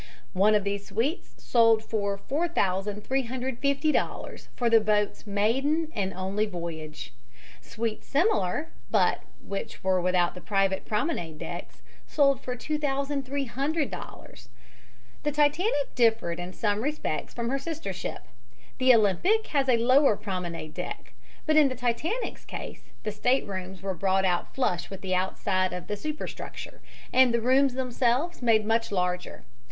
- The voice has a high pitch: Yes, high, 230 Hz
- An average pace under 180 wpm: Yes, average, 140 wpm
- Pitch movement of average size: No, wide, 6.1 semitones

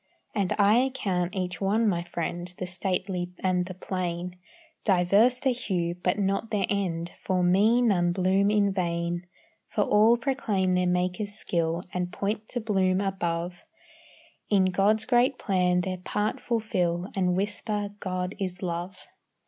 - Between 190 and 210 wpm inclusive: No, average, 150 wpm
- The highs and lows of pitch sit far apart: No, narrow, 2.6 semitones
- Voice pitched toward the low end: No, medium, 185 Hz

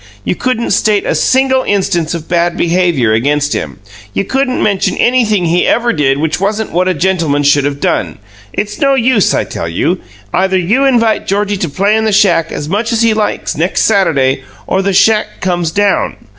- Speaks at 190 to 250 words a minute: Yes, average, 195 wpm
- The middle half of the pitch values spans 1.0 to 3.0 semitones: No, average, 4.8 semitones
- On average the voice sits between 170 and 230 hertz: Yes, high, 190 Hz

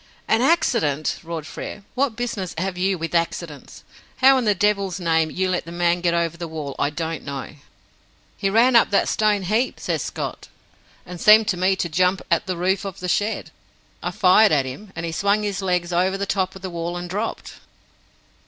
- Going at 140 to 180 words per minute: No, fast, 205 wpm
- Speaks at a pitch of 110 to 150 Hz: No, medium, 185 Hz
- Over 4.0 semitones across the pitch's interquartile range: No, average, 3.3 semitones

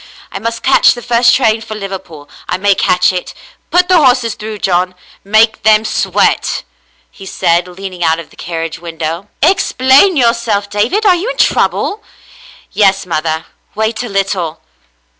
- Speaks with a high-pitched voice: Yes, high, 205 Hz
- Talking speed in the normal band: Yes, average, 175 wpm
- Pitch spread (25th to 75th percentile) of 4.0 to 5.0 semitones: Yes, average, 4.6 semitones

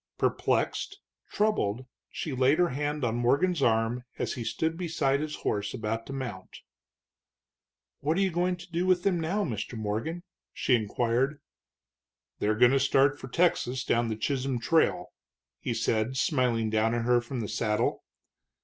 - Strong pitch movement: Yes, wide, 5.9 semitones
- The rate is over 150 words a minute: Yes, average, 160 wpm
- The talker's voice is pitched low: Yes, low, 130 Hz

